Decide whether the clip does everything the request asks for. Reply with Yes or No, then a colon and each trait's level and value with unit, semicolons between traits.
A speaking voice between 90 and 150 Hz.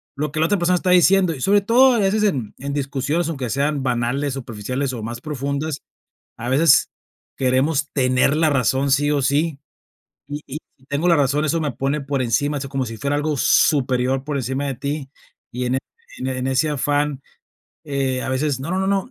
Yes: medium, 140 Hz